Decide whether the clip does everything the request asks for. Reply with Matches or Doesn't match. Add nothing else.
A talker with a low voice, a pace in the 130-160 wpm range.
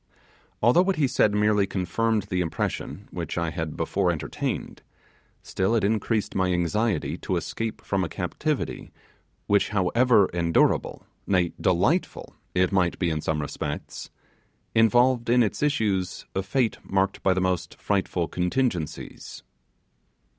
Matches